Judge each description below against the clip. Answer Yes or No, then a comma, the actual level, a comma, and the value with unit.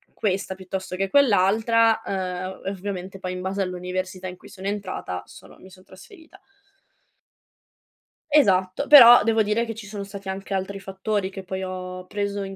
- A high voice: Yes, high, 195 Hz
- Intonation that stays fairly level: Yes, narrow, 1.9 semitones